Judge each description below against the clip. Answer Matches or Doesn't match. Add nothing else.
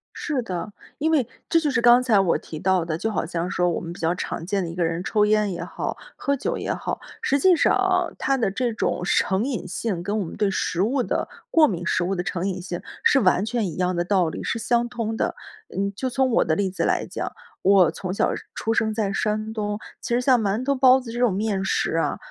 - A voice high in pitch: Matches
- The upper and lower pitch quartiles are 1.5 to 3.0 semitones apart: Doesn't match